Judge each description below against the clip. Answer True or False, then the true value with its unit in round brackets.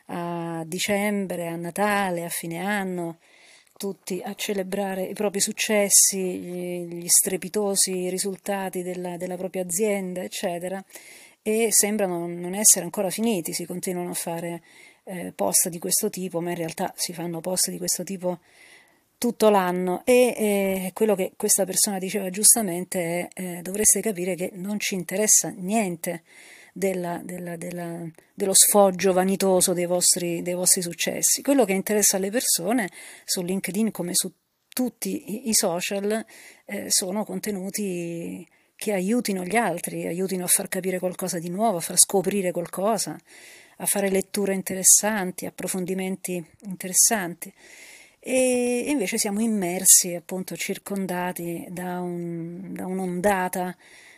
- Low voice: False (185 Hz)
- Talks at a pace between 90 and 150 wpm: True (135 wpm)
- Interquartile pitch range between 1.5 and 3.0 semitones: True (2.4 semitones)